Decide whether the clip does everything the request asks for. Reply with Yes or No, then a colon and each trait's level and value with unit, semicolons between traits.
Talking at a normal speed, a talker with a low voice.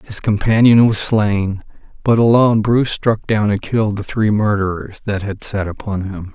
Yes: average, 180 wpm; low, 105 Hz